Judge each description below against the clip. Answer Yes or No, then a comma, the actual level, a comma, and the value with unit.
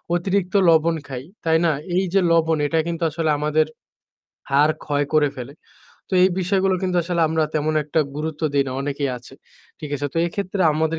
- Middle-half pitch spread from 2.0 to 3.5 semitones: Yes, average, 2.8 semitones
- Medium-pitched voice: Yes, medium, 160 Hz